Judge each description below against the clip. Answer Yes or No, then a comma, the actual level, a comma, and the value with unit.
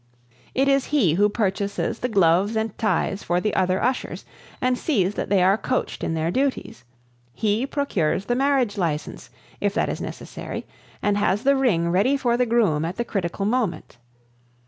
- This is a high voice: Yes, high, 205 Hz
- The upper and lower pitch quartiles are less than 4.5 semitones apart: No, average, 5.3 semitones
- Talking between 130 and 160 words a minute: No, average, 175 wpm